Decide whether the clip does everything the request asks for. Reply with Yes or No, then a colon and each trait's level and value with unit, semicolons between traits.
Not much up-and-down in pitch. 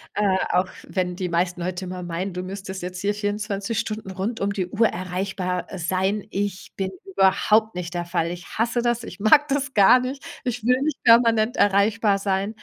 No: average, 3.3 semitones